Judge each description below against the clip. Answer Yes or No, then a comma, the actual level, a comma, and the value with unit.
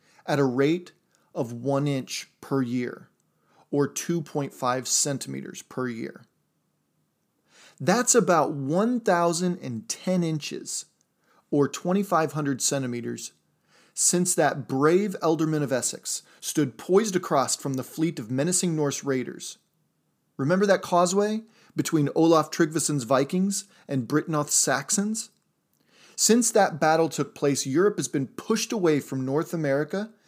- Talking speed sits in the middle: No, slow, 115 wpm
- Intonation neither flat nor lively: Yes, average, 4.6 semitones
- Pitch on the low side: No, medium, 155 Hz